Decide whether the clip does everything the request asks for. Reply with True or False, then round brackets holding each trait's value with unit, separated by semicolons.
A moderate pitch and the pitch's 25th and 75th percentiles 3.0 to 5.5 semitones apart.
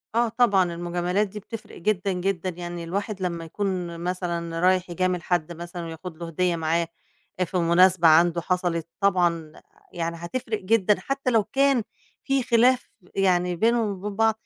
True (180 Hz; 3.4 semitones)